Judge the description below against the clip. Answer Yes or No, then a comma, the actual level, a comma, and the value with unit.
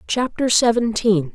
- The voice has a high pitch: Yes, high, 220 Hz